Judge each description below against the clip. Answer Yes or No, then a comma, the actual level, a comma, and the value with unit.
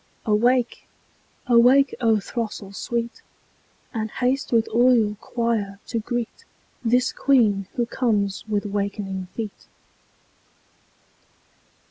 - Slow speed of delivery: Yes, slow, 100 wpm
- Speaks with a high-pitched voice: Yes, high, 230 Hz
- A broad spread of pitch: No, average, 2.9 semitones